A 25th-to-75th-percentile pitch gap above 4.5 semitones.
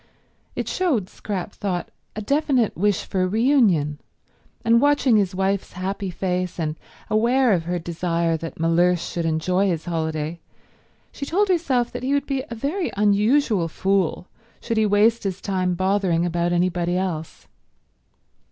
Yes: average, 5.0 semitones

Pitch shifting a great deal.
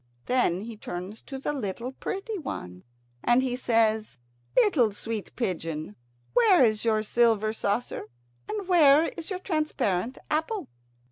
Yes: wide, 6.5 semitones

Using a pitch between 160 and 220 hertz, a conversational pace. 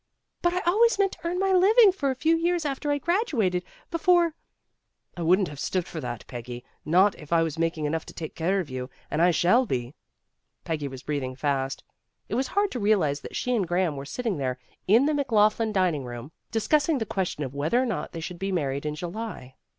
No: medium, 185 Hz; fast, 220 wpm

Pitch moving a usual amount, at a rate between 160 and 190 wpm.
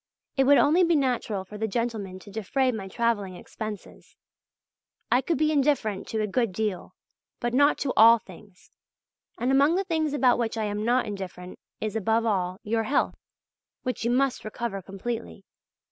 Yes: average, 4.3 semitones; average, 175 wpm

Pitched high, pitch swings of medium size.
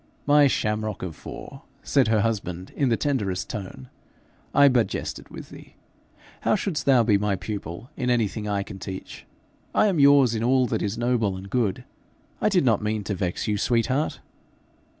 No: low, 110 Hz; average, 4.5 semitones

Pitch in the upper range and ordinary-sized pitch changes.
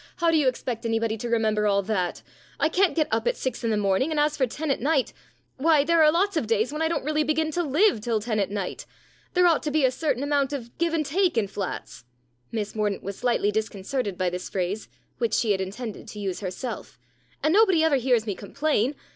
No: very high, 250 Hz; wide, 6.7 semitones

